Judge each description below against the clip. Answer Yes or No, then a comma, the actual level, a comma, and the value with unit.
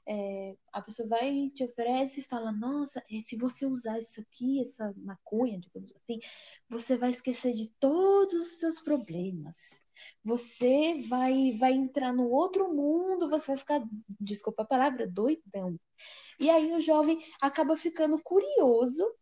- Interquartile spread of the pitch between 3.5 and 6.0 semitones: Yes, average, 5.0 semitones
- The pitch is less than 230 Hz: No, very high, 255 Hz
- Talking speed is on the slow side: No, average, 145 wpm